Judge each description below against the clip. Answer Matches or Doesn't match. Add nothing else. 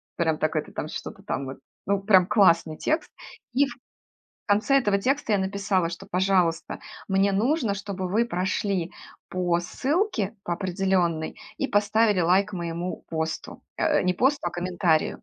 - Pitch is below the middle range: Doesn't match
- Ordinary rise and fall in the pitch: Matches